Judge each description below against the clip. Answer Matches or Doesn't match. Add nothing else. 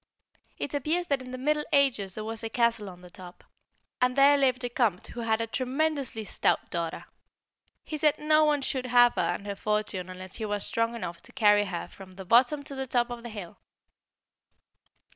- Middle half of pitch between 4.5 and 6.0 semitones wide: Matches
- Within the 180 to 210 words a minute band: Matches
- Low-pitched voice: Doesn't match